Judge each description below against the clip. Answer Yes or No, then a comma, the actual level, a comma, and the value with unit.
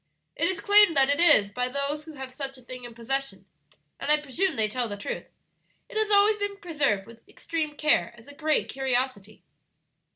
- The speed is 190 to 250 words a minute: Yes, average, 200 wpm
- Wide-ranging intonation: No, average, 4.6 semitones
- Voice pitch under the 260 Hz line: No, very high, 280 Hz